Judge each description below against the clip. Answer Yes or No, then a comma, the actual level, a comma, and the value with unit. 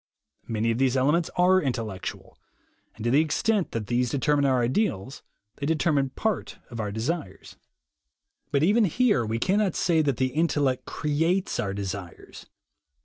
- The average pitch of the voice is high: No, medium, 140 Hz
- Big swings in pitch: Yes, wide, 6.2 semitones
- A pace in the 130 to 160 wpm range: Yes, average, 155 wpm